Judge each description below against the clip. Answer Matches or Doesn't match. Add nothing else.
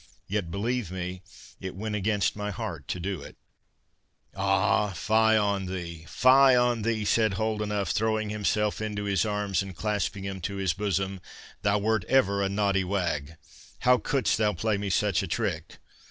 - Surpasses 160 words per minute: Matches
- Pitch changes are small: Matches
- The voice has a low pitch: Matches